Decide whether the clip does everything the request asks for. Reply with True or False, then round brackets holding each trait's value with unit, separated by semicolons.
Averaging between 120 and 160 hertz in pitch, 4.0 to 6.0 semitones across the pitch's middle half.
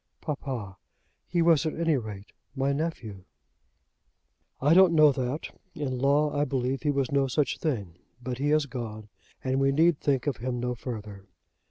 False (135 Hz; 3.4 semitones)